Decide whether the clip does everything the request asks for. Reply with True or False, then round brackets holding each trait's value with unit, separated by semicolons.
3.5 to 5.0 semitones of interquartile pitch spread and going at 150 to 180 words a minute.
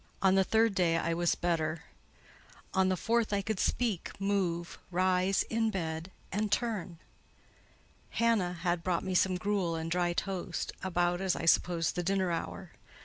False (2.4 semitones; 160 wpm)